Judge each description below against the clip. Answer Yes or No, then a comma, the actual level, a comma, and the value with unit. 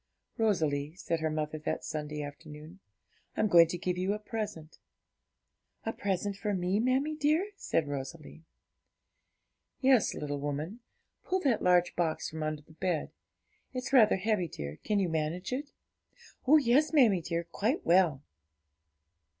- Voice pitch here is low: No, medium, 180 Hz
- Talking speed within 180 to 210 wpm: No, average, 145 wpm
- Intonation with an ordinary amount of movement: No, wide, 6.3 semitones